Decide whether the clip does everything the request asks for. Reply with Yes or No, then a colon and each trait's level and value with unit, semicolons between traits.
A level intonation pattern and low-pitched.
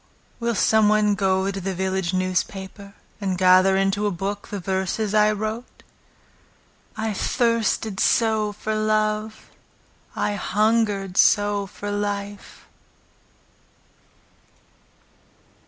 No: narrow, 1.9 semitones; high, 205 Hz